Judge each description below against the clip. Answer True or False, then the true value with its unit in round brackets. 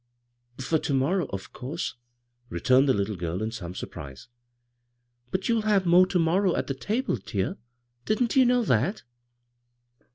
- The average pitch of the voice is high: False (135 Hz)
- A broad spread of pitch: True (8.8 semitones)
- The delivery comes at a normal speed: True (165 wpm)